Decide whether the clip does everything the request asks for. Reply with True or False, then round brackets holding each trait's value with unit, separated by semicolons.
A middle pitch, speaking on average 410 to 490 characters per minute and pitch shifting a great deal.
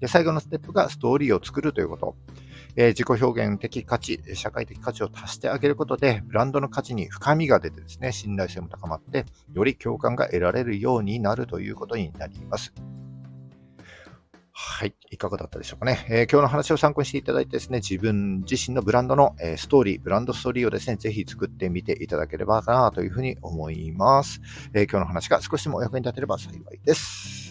False (115 Hz; 440 characters per minute; 5.8 semitones)